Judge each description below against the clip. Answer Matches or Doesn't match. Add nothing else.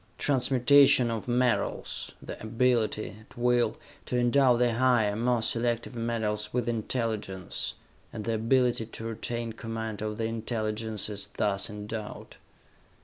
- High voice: Doesn't match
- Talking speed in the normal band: Doesn't match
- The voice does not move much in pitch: Matches